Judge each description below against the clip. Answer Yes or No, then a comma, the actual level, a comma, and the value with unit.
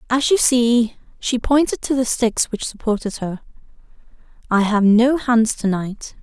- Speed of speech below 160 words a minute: Yes, average, 145 wpm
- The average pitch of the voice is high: Yes, high, 235 Hz